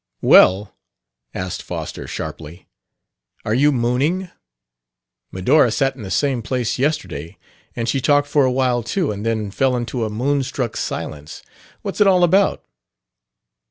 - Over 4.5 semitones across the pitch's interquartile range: Yes, average, 5.0 semitones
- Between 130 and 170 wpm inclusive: Yes, slow, 135 wpm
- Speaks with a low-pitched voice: Yes, low, 125 Hz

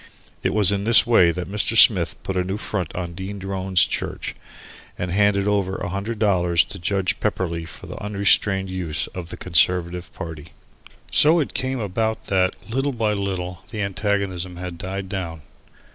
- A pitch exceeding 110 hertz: No, very low, 95 Hz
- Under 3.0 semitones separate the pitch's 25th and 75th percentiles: Yes, narrow, 2.5 semitones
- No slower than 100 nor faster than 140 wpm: No, average, 175 wpm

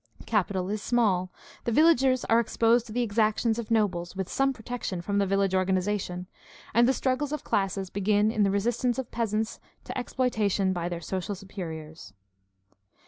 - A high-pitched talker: Yes, high, 210 Hz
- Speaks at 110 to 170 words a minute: Yes, average, 165 wpm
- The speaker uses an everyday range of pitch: Yes, average, 3.9 semitones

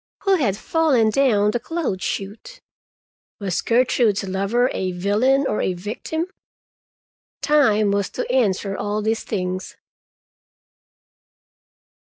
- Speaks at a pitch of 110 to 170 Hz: No, high, 215 Hz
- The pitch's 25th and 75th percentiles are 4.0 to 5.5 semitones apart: Yes, average, 4.7 semitones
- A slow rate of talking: Yes, slow, 110 wpm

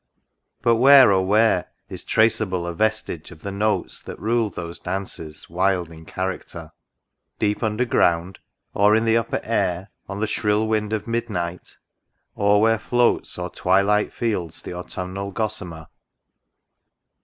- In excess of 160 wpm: No, average, 150 wpm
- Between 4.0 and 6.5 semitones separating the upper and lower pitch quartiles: No, average, 3.6 semitones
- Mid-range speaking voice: No, low, 100 Hz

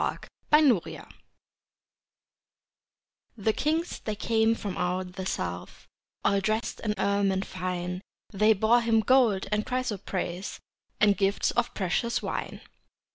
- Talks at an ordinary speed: No, slow, 120 wpm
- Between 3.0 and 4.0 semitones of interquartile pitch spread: Yes, average, 3.3 semitones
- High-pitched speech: Yes, high, 205 Hz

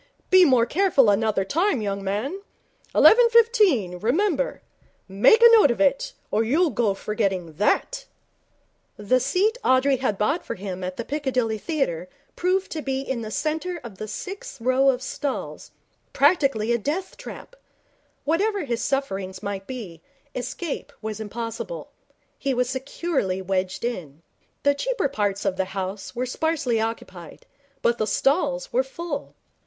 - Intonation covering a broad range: Yes, wide, 7.8 semitones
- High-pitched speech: Yes, very high, 255 Hz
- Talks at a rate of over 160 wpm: No, average, 150 wpm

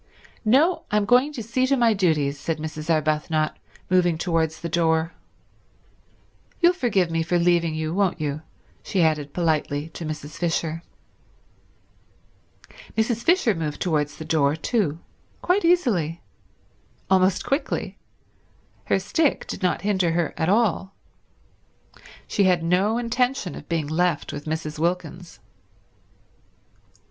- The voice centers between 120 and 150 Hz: No, medium, 170 Hz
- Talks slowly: Yes, slow, 130 wpm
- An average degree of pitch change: Yes, average, 5.0 semitones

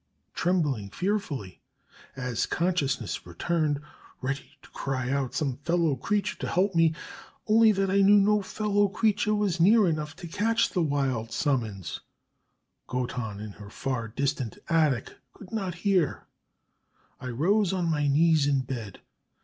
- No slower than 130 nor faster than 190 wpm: Yes, average, 145 wpm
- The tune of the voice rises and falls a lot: Yes, wide, 7.0 semitones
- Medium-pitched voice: Yes, medium, 155 Hz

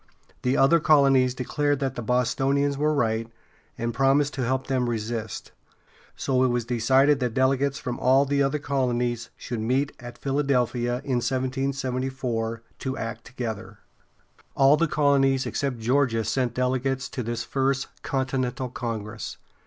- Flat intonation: Yes, narrow, 2.3 semitones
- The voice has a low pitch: Yes, low, 130 Hz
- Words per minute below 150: Yes, average, 140 wpm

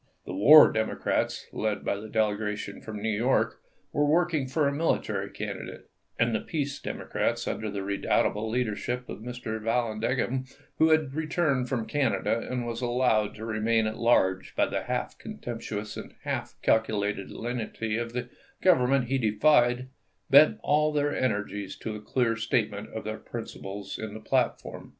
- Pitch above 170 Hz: No, low, 115 Hz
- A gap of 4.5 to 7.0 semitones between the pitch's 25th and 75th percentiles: No, average, 3.6 semitones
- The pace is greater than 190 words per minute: No, average, 160 wpm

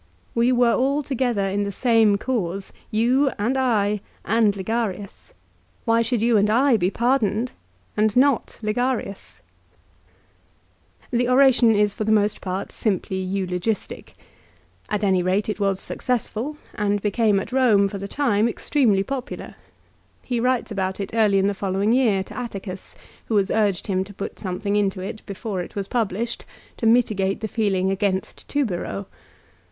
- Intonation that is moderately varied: Yes, average, 3.4 semitones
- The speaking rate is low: No, average, 160 wpm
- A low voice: No, high, 210 Hz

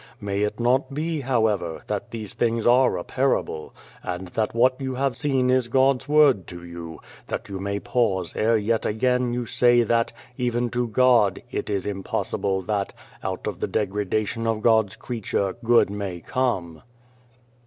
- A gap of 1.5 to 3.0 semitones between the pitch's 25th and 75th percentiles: No, average, 4.1 semitones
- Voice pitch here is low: Yes, low, 115 Hz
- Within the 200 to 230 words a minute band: No, average, 165 wpm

